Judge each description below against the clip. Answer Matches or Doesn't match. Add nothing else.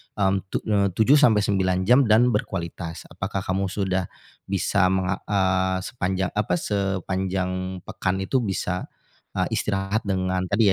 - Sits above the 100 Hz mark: Doesn't match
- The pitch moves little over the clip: Matches